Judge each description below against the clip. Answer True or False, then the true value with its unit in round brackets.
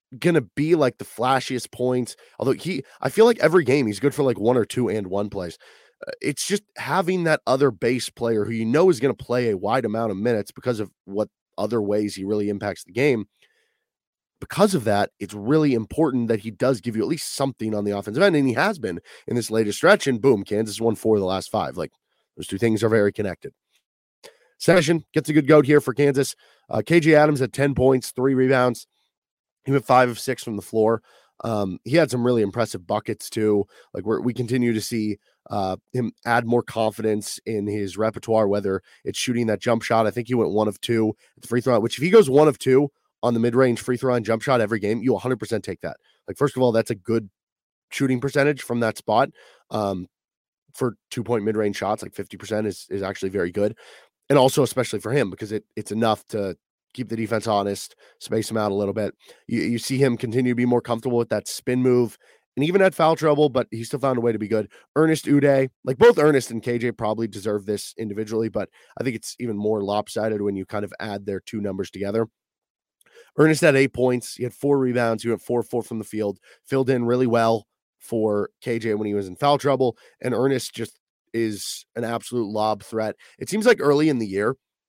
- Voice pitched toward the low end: True (115 Hz)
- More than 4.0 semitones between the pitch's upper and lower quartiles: False (3.7 semitones)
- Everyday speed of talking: False (225 wpm)